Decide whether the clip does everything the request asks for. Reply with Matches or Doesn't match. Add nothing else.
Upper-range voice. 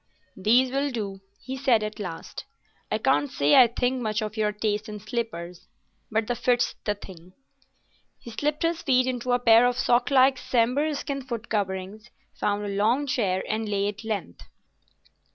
Matches